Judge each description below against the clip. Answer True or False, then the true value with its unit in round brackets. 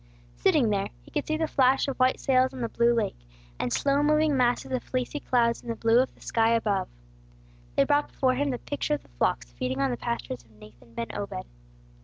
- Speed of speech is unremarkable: False (225 wpm)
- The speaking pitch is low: False (235 Hz)